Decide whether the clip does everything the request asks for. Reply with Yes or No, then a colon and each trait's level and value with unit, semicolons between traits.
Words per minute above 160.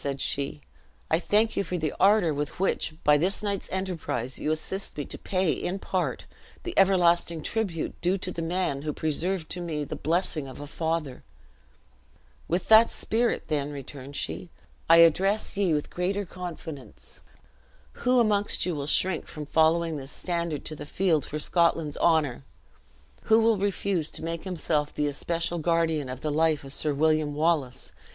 Yes: average, 170 wpm